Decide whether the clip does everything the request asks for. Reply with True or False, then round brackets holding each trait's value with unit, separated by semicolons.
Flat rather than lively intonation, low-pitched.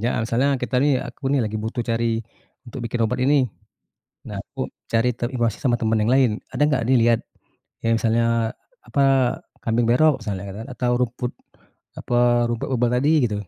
True (1.9 semitones; 120 Hz)